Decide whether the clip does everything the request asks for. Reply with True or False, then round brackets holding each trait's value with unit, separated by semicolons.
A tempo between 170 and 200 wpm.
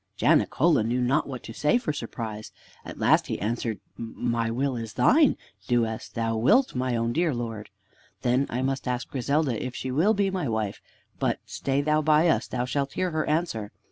True (195 wpm)